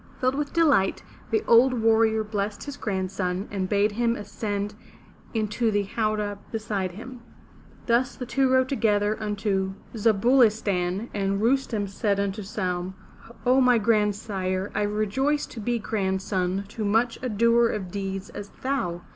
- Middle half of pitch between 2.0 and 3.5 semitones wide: Yes, average, 3.0 semitones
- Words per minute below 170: Yes, average, 155 wpm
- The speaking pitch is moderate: No, high, 210 Hz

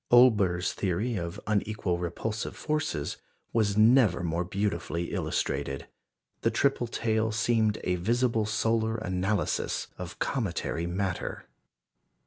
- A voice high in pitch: No, low, 105 Hz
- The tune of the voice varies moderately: Yes, average, 4.2 semitones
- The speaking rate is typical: No, slow, 110 wpm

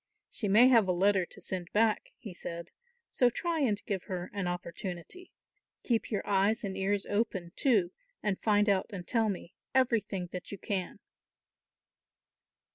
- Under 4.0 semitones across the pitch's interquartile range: Yes, average, 3.4 semitones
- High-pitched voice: Yes, high, 200 Hz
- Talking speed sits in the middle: Yes, average, 160 wpm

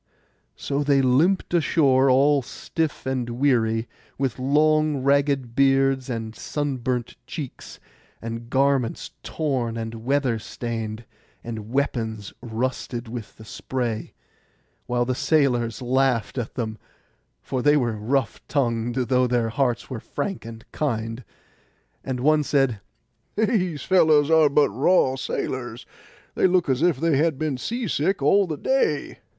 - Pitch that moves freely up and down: No, average, 3.7 semitones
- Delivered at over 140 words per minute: No, slow, 135 wpm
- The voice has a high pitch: No, low, 130 Hz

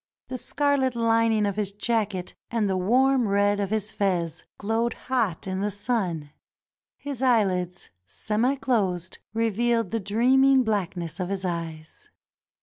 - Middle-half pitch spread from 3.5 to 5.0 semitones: Yes, average, 4.1 semitones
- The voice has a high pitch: Yes, high, 210 Hz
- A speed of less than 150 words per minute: Yes, average, 140 wpm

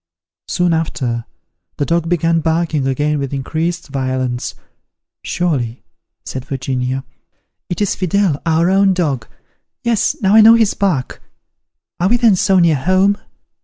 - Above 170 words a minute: No, slow, 135 wpm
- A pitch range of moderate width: No, wide, 5.7 semitones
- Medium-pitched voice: Yes, medium, 165 Hz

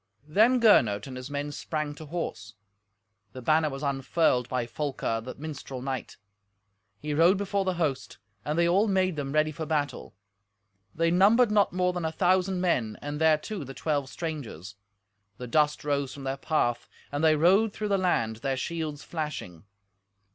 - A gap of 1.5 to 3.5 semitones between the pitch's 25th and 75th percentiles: No, average, 4.6 semitones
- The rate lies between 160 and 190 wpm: Yes, average, 170 wpm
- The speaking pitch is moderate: Yes, medium, 155 Hz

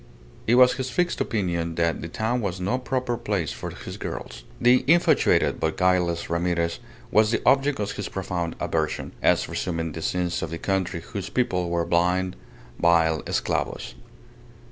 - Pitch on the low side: Yes, very low, 90 Hz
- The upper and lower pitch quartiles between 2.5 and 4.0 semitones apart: No, average, 5.0 semitones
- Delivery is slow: No, average, 165 wpm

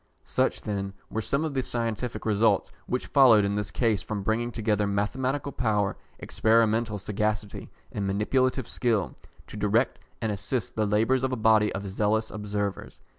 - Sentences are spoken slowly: No, average, 160 wpm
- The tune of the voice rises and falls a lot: No, narrow, 2.5 semitones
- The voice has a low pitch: Yes, low, 110 Hz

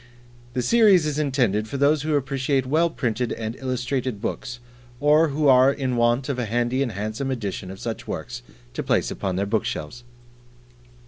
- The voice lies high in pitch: No, low, 130 Hz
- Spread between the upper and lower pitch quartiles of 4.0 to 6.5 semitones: No, average, 3.6 semitones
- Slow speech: No, average, 175 wpm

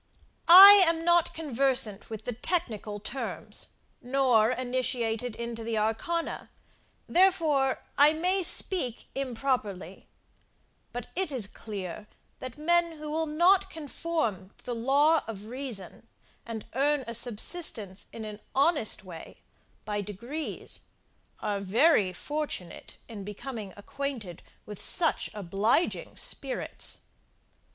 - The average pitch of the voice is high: Yes, very high, 250 Hz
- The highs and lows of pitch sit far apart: Yes, wide, 6.7 semitones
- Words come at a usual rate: No, slow, 115 wpm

